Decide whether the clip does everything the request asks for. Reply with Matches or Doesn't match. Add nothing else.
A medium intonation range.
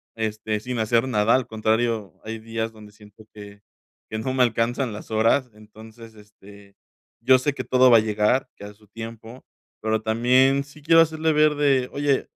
Matches